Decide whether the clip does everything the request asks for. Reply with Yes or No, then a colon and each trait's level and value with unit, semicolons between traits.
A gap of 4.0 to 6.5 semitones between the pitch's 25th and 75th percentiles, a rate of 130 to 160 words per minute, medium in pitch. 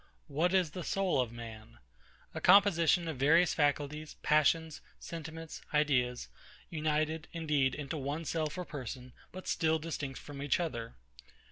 No: average, 3.1 semitones; average, 140 wpm; medium, 155 Hz